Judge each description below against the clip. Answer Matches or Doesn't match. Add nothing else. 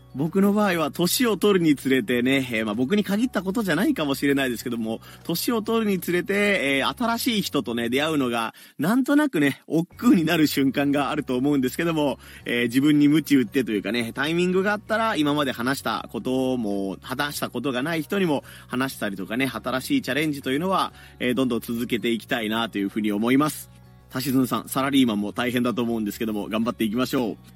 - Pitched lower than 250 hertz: Matches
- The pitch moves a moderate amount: Doesn't match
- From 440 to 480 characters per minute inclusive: Matches